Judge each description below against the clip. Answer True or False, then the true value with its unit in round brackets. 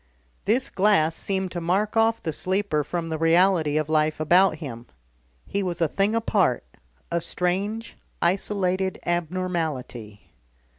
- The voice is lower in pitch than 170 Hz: False (180 Hz)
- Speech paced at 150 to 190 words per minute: False (135 wpm)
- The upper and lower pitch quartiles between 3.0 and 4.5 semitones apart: True (3.8 semitones)